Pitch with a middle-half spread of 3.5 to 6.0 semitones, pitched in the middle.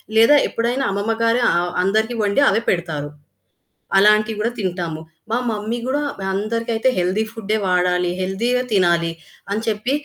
No: average, 3.9 semitones; high, 210 Hz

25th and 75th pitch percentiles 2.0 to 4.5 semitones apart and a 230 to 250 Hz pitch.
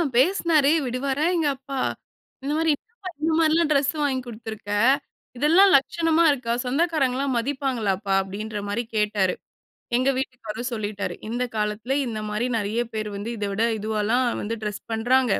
No: average, 4.9 semitones; high, 245 Hz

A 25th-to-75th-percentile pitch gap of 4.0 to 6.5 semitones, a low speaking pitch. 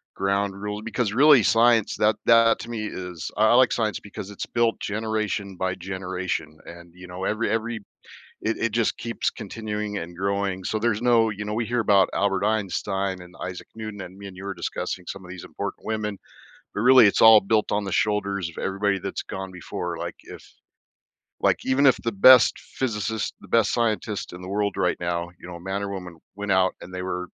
No: average, 2.9 semitones; low, 100 Hz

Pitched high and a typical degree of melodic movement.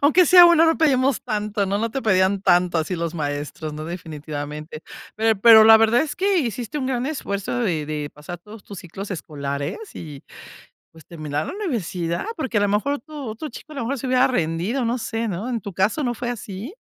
No: high, 210 Hz; wide, 7.2 semitones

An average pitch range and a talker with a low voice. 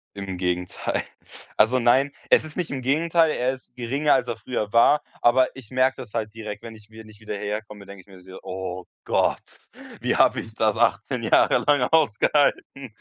Yes: average, 4.2 semitones; low, 115 Hz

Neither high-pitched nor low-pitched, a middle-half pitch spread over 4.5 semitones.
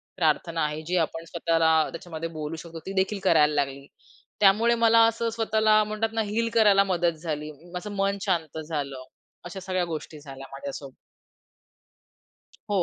Yes: medium, 170 Hz; average, 5.1 semitones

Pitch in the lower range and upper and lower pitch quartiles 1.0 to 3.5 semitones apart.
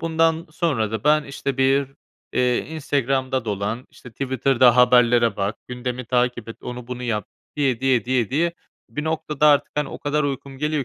Yes: low, 130 Hz; average, 3.1 semitones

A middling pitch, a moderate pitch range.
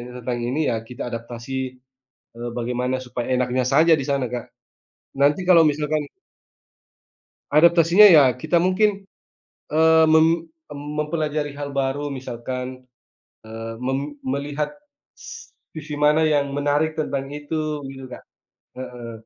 Yes: medium, 145 Hz; average, 3.3 semitones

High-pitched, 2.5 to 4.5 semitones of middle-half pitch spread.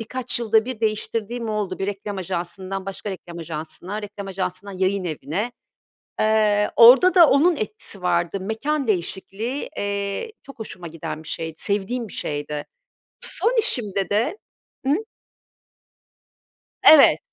Yes: high, 205 Hz; average, 3.8 semitones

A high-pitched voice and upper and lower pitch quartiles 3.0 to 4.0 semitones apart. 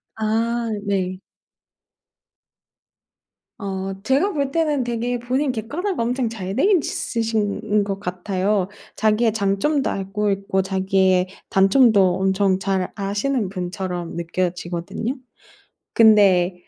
Yes: high, 200 Hz; average, 3.7 semitones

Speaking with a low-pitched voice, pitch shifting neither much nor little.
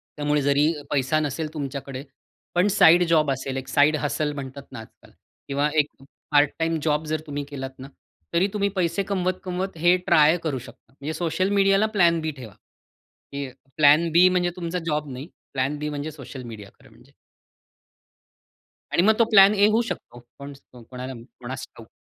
No: medium, 150 Hz; average, 4.0 semitones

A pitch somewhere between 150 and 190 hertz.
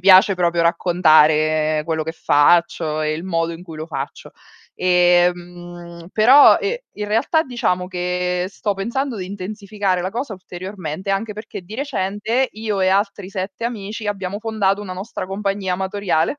Yes: medium, 185 Hz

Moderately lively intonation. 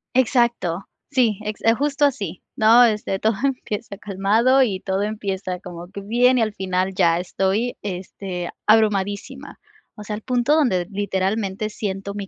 Yes: average, 3.5 semitones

